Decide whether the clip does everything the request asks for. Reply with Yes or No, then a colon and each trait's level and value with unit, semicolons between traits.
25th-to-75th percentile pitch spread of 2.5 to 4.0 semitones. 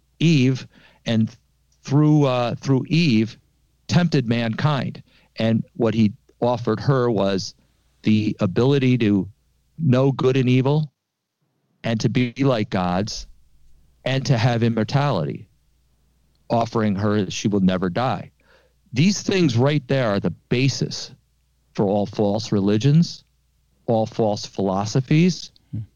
No: average, 5.2 semitones